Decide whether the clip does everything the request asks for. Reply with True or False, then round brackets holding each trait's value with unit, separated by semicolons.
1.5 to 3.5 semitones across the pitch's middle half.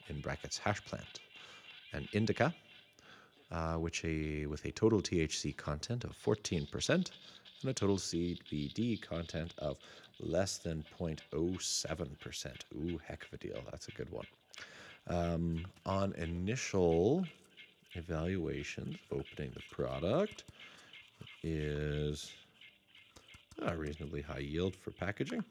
False (4.4 semitones)